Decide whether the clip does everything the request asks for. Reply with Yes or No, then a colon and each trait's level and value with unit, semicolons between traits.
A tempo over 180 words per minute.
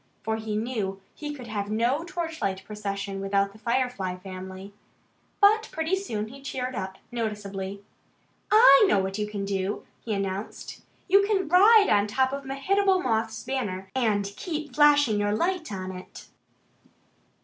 No: average, 150 wpm